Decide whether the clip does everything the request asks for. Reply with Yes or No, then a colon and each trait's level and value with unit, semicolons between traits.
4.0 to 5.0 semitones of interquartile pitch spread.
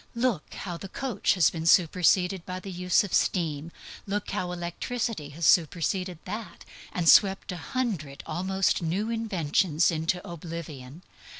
No: average, 3.0 semitones